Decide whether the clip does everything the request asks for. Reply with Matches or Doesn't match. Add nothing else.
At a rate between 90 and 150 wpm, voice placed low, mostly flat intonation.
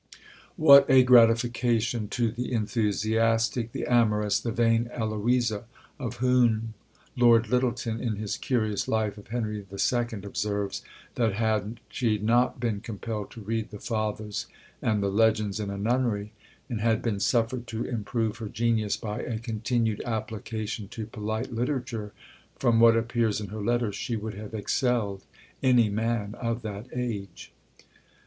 Matches